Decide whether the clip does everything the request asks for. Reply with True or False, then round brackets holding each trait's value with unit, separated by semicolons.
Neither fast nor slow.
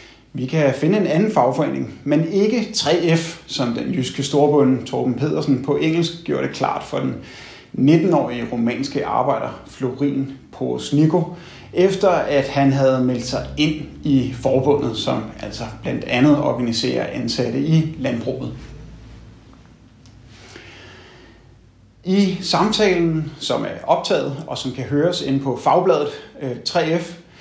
False (125 wpm)